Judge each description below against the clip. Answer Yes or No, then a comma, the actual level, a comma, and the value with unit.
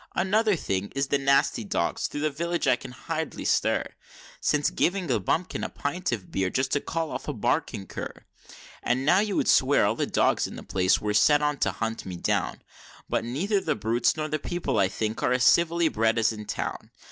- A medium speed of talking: No, fast, 215 wpm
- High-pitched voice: No, low, 135 Hz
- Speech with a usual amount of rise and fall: No, wide, 6.8 semitones